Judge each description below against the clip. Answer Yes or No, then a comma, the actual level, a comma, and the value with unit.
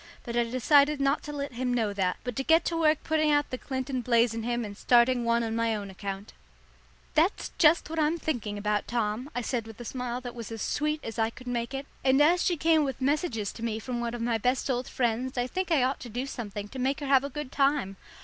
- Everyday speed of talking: No, fast, 255 wpm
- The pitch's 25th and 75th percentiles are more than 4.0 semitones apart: No, average, 3.7 semitones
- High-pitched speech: Yes, very high, 250 Hz